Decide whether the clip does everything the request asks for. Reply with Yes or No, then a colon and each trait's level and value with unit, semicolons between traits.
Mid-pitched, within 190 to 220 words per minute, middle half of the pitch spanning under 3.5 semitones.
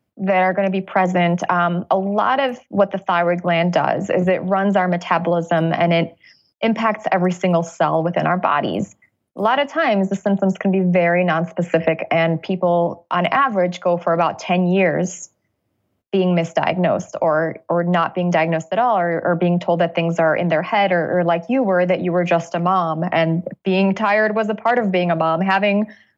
Yes: medium, 180 Hz; fast, 205 wpm; narrow, 2.4 semitones